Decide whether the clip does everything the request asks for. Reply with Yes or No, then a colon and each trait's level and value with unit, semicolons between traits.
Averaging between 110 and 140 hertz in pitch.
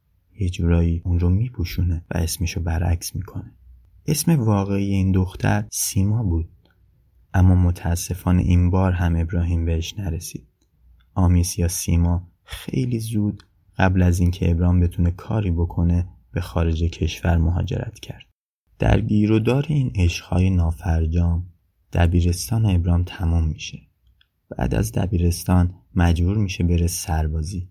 No: very low, 90 Hz